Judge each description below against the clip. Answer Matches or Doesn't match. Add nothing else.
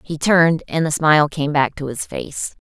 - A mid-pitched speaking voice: Matches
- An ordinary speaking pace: Doesn't match